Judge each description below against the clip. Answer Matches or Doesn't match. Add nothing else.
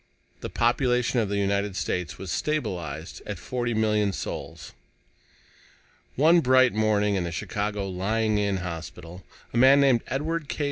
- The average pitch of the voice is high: Doesn't match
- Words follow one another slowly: Doesn't match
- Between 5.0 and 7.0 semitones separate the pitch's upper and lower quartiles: Doesn't match